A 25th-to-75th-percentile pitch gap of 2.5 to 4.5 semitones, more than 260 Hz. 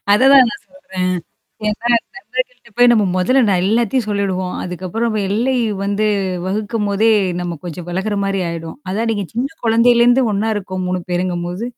No: average, 4.1 semitones; high, 205 Hz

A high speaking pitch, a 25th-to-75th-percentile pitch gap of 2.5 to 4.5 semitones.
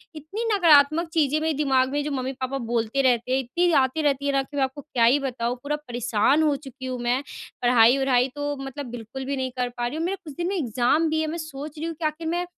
Yes: very high, 275 Hz; average, 3.4 semitones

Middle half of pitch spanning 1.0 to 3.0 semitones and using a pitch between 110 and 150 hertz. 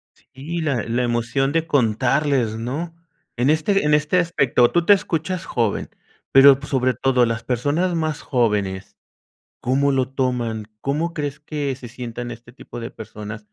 No: average, 4.2 semitones; low, 135 Hz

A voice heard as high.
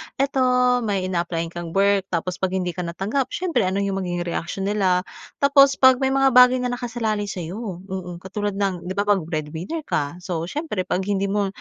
Yes: high, 195 Hz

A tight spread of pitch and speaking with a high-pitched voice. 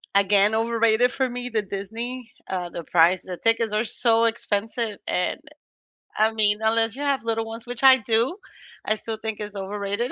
Yes: narrow, 2.2 semitones; high, 225 Hz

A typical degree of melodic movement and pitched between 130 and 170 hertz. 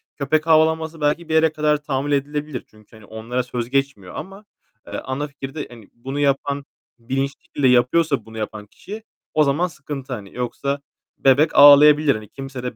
Yes: average, 3.3 semitones; medium, 140 Hz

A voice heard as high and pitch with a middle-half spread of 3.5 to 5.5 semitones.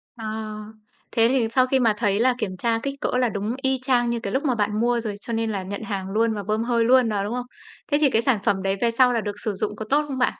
No: high, 230 Hz; average, 3.1 semitones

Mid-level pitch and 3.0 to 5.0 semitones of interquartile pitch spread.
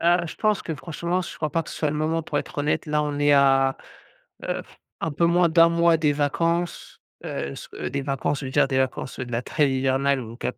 Yes: medium, 150 Hz; average, 3.6 semitones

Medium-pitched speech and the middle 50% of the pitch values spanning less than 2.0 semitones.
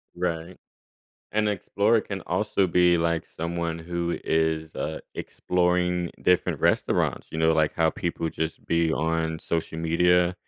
No: very low, 85 Hz; narrow, 1.6 semitones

